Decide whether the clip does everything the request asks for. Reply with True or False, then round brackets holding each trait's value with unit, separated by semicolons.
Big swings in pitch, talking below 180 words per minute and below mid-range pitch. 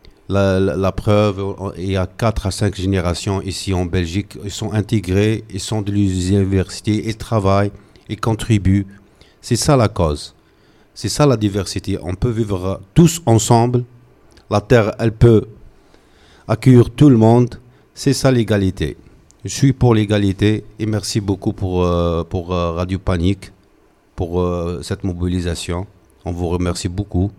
False (3.0 semitones; 150 wpm; 100 Hz)